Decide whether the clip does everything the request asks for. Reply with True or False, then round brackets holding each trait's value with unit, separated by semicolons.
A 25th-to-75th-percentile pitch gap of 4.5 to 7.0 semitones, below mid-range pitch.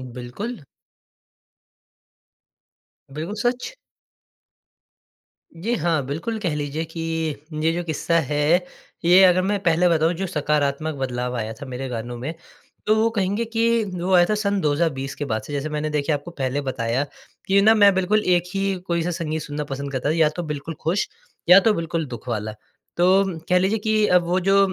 False (5.0 semitones; 165 Hz)